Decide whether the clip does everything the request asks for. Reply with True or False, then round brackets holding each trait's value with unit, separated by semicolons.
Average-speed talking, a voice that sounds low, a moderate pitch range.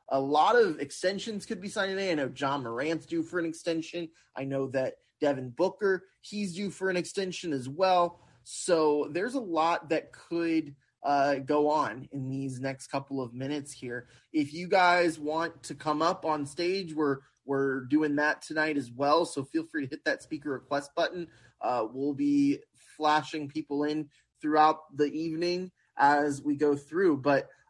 False (180 wpm; 155 Hz; 3.7 semitones)